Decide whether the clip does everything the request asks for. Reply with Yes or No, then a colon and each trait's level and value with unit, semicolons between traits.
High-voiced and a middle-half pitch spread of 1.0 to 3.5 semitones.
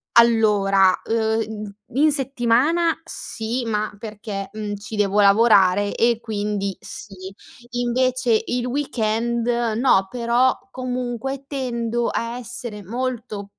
Yes: high, 230 Hz; average, 2.9 semitones